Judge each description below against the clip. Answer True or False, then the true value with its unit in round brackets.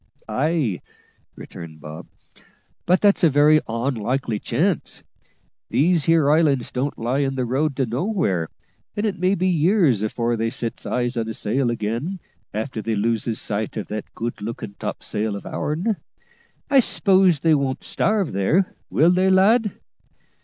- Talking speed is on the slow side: False (155 wpm)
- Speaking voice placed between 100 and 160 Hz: True (135 Hz)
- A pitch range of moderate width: False (7.6 semitones)